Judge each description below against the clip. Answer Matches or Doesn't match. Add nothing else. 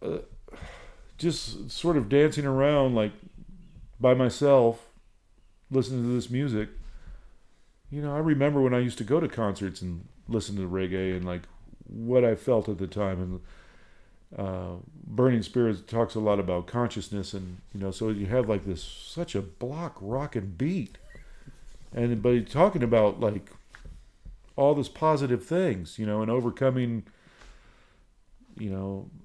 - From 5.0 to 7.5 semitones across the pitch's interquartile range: Matches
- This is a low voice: Matches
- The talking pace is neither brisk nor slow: Matches